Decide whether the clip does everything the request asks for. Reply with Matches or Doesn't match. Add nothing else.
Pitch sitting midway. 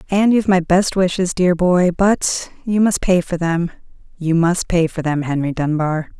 Matches